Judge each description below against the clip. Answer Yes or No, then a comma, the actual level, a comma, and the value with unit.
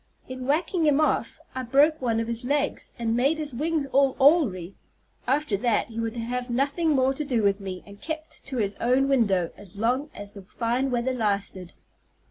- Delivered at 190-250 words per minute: Yes, average, 195 wpm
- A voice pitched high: Yes, very high, 250 Hz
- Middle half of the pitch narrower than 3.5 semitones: No, average, 4.1 semitones